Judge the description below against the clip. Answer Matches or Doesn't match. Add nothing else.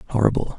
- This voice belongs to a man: Matches